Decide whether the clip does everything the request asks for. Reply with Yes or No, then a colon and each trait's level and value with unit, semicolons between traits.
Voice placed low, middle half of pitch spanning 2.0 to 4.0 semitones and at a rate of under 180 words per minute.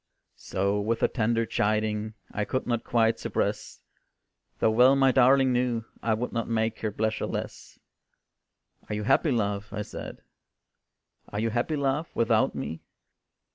Yes: low, 115 Hz; narrow, 2.5 semitones; average, 150 wpm